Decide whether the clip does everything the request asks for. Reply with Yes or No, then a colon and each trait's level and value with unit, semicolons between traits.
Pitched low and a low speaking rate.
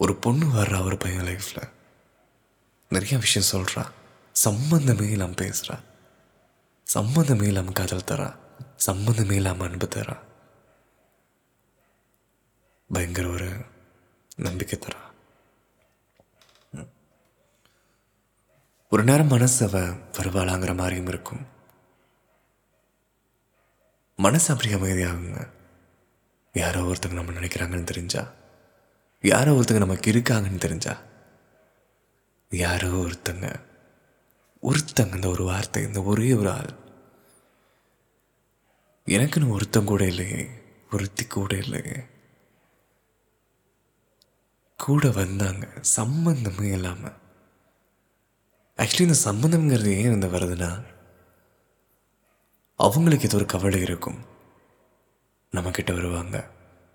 No: low, 100 Hz; average, 85 wpm